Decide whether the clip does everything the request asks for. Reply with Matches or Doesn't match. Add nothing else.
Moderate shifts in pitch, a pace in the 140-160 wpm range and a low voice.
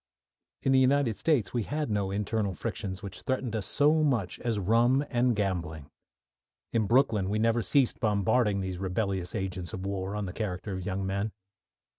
Doesn't match